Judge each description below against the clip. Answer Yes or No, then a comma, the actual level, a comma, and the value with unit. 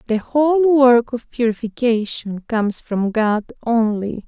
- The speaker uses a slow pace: Yes, slow, 125 wpm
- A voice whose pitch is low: No, high, 235 Hz